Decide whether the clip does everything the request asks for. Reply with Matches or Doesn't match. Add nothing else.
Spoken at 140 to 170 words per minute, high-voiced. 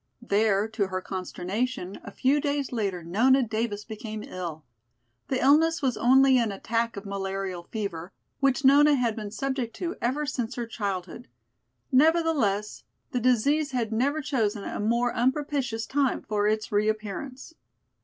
Matches